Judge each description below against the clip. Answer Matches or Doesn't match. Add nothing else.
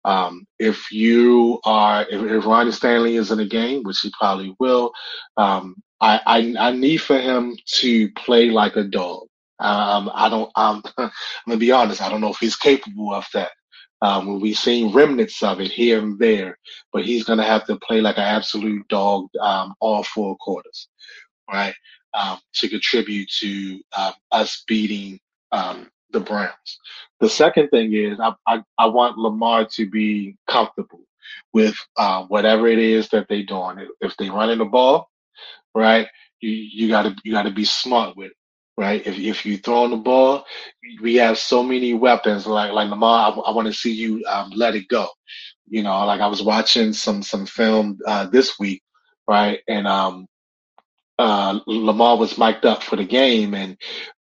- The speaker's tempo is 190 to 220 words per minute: Doesn't match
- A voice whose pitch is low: Matches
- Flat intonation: Matches